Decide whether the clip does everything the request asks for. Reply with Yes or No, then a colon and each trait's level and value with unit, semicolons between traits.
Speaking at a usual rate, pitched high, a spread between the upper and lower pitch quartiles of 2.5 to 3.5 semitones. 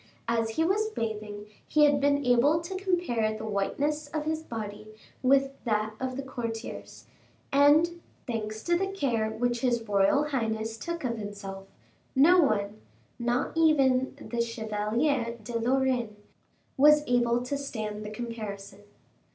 No: average, 145 wpm; high, 240 Hz; average, 4.8 semitones